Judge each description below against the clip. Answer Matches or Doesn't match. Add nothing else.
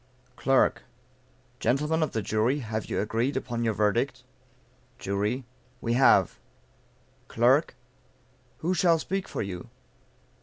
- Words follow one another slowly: Matches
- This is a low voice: Matches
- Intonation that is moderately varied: Matches